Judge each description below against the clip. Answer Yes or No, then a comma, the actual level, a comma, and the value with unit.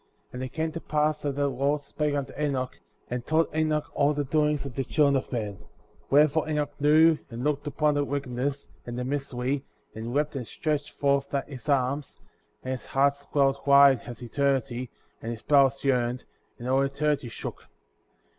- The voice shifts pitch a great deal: No, narrow, 2.4 semitones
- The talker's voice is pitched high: No, medium, 140 Hz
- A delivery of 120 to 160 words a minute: No, average, 185 wpm